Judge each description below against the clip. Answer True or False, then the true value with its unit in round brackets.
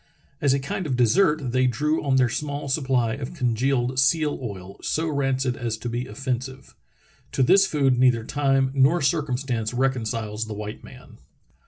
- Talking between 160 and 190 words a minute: True (165 wpm)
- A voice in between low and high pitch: False (130 Hz)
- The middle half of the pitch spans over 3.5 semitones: False (2.8 semitones)